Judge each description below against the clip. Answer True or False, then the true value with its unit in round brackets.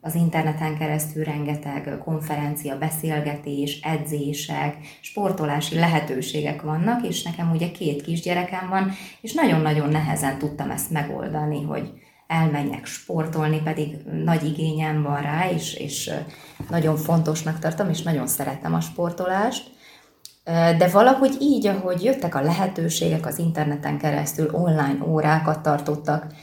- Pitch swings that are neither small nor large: False (2.3 semitones)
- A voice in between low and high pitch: True (155 Hz)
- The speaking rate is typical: True (120 wpm)